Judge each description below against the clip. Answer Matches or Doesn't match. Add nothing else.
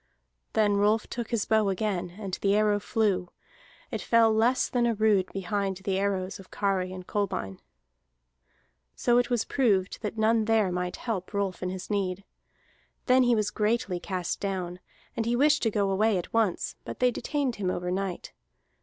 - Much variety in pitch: Doesn't match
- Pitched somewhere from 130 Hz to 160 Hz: Doesn't match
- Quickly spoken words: Doesn't match